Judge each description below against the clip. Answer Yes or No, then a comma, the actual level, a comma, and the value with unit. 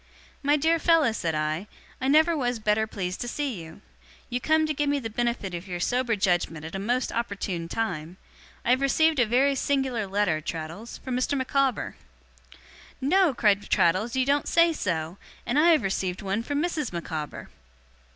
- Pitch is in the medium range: No, high, 235 Hz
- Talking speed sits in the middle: Yes, average, 180 wpm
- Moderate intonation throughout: No, wide, 7.1 semitones